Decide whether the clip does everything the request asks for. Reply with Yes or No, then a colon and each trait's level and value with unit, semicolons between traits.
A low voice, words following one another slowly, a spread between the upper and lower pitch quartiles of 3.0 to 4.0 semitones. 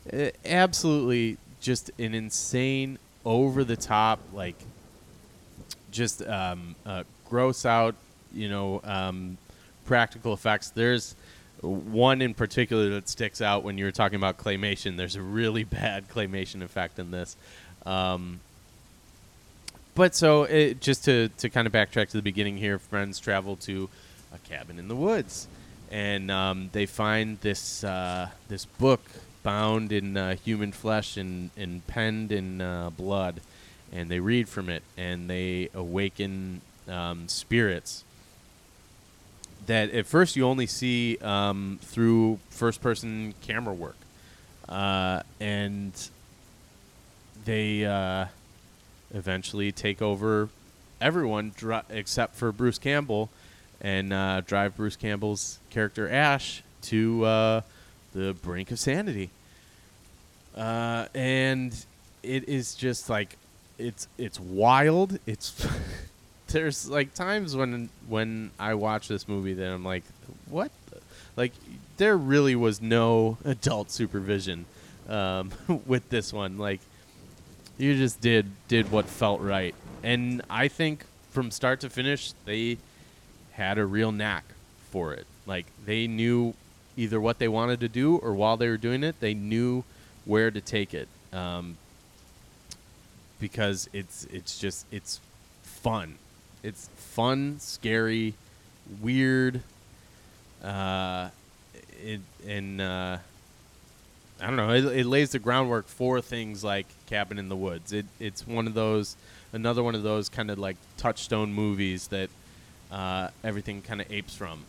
Yes: low, 105 Hz; slow, 130 wpm; average, 3.4 semitones